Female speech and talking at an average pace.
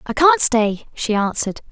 Yes: female; average, 175 wpm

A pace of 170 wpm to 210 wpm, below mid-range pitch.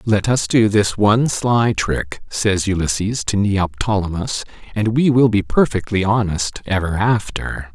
No: average, 145 wpm; low, 105 Hz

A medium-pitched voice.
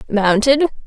No: high, 240 Hz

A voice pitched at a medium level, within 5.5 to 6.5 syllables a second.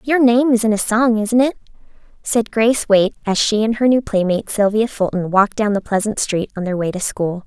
No: high, 215 Hz; 5.7 syllables/s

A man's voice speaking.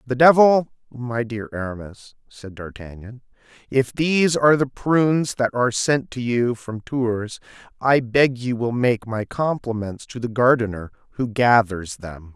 Yes: male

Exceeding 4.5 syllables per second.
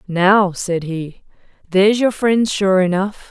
No: 3.7 syllables/s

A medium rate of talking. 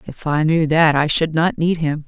No: fast, 260 wpm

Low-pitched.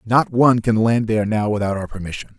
Yes: low, 110 Hz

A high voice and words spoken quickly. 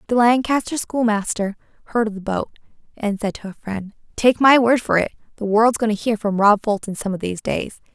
Yes: high, 220 Hz; fast, 220 wpm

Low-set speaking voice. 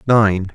Yes: low, 100 Hz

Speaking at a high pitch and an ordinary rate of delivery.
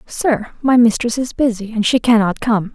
Yes: high, 230 Hz; average, 195 wpm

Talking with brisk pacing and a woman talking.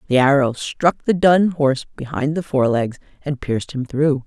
No: average, 185 wpm; female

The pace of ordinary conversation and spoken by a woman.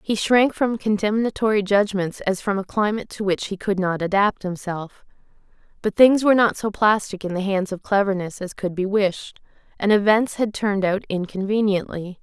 Yes: average, 180 wpm; female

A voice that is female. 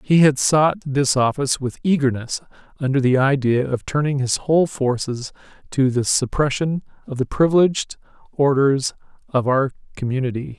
No: male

